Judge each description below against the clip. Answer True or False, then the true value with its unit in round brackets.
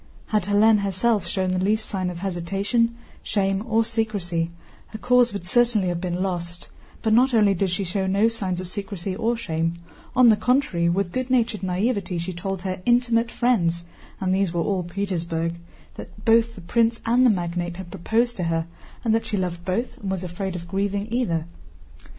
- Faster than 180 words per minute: True (190 wpm)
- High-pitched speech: True (195 Hz)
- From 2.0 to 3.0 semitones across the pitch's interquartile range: False (4.2 semitones)